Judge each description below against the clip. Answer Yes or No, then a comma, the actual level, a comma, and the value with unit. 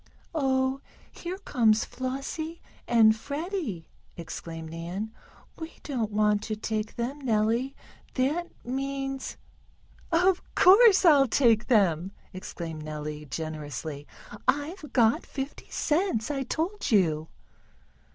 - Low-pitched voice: No, high, 240 Hz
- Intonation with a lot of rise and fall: Yes, wide, 7.2 semitones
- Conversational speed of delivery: No, slow, 110 wpm